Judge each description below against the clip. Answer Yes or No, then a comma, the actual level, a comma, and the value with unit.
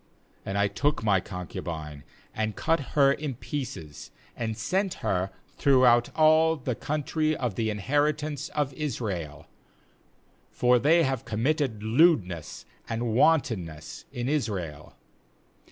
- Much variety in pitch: Yes, wide, 6.8 semitones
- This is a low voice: Yes, low, 120 Hz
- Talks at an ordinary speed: No, slow, 120 wpm